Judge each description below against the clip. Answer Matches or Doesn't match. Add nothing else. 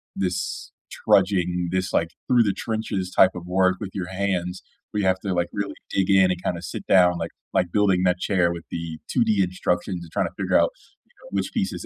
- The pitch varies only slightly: Matches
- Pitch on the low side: Matches